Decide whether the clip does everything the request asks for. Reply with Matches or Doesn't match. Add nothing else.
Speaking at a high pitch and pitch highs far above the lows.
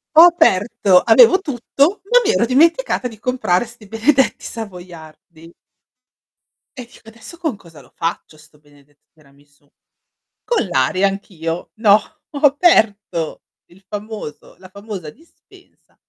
Matches